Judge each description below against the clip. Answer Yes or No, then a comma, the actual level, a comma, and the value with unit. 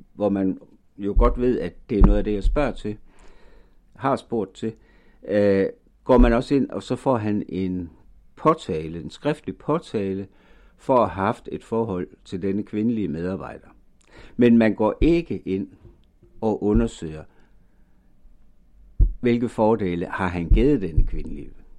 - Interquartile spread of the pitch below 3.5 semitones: No, average, 3.8 semitones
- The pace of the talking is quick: No, average, 150 wpm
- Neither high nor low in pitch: No, low, 105 Hz